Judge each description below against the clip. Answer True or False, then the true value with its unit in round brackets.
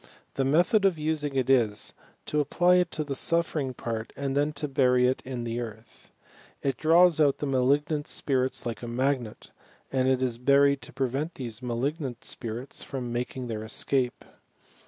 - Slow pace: False (175 wpm)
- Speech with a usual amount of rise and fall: True (3.1 semitones)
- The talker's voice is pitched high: False (135 Hz)